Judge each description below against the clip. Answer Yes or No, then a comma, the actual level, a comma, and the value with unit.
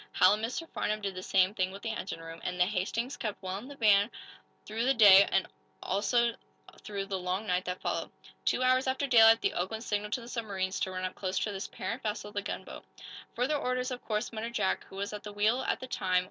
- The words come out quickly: Yes, fast, 240 wpm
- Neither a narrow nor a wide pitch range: Yes, average, 3.6 semitones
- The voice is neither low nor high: No, high, 210 Hz